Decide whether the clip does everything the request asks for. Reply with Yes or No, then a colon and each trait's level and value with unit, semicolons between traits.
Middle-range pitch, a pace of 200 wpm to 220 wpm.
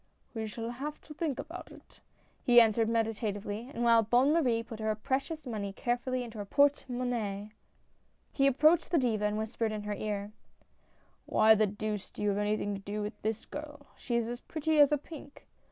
No: high, 230 Hz; fast, 205 wpm